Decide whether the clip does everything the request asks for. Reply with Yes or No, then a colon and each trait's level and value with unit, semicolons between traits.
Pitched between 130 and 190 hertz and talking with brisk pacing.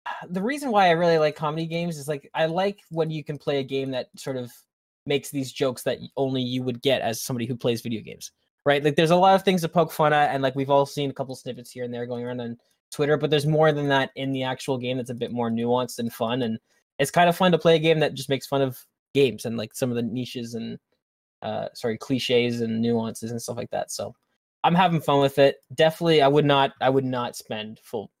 Yes: low, 135 Hz; fast, 260 wpm